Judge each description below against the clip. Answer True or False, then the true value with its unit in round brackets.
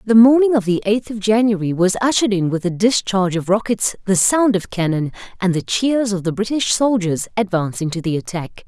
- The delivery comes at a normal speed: False (210 wpm)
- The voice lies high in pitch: True (200 Hz)